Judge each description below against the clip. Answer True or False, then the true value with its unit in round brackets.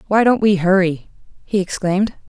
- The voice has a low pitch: False (195 Hz)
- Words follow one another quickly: False (150 wpm)